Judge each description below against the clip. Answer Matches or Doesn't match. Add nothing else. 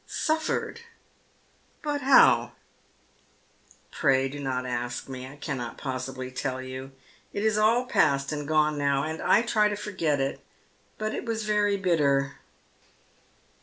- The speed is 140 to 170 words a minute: Matches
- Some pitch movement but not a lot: Doesn't match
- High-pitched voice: Doesn't match